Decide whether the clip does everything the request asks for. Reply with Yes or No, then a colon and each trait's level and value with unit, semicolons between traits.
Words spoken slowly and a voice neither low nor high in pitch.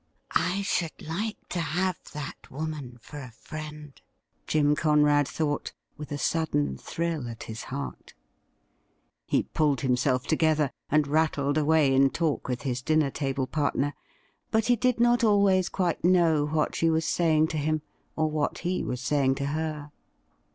No: average, 160 wpm; medium, 150 Hz